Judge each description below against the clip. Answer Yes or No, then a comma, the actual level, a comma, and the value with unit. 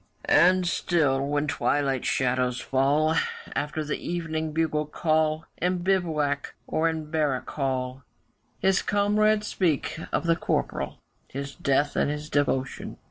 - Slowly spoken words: Yes, slow, 130 wpm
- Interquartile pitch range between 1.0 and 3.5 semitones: Yes, average, 3.1 semitones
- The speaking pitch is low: No, medium, 155 Hz